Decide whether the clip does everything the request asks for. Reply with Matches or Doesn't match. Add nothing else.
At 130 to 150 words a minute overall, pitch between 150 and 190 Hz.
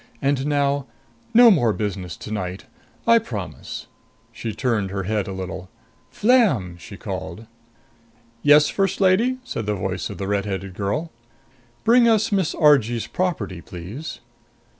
Doesn't match